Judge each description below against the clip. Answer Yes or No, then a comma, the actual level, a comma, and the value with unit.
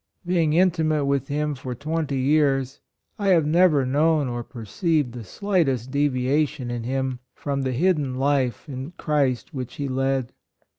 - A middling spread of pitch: Yes, average, 3.2 semitones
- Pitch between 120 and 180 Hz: Yes, medium, 140 Hz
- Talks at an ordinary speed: Yes, average, 150 wpm